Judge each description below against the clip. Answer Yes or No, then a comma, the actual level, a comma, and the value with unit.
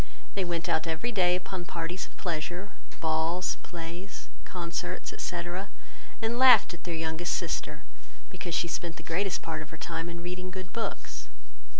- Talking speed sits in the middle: Yes, average, 165 wpm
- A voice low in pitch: No, medium, 175 Hz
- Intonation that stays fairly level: Yes, narrow, 1.9 semitones